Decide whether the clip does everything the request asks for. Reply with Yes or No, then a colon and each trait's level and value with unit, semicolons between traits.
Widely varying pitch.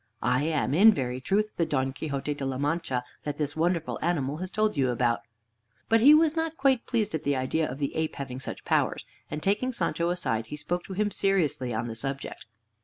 Yes: wide, 6.6 semitones